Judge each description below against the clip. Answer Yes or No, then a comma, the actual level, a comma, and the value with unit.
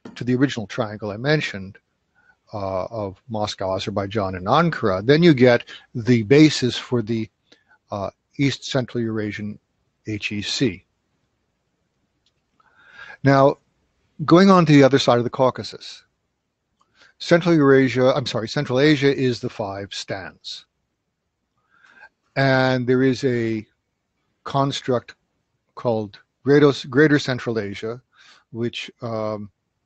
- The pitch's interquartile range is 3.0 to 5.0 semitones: Yes, average, 4.2 semitones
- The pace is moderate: No, slow, 110 wpm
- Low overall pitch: Yes, low, 125 Hz